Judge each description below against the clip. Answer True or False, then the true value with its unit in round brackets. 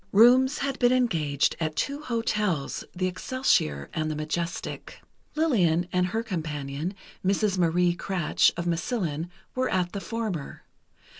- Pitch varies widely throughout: True (6.2 semitones)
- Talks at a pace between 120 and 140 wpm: True (135 wpm)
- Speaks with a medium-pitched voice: True (180 Hz)